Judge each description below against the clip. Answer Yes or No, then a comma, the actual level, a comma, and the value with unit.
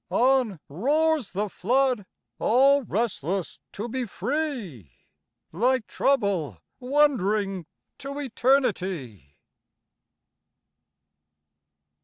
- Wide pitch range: Yes, wide, 6.2 semitones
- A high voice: Yes, high, 230 Hz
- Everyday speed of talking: No, slow, 70 wpm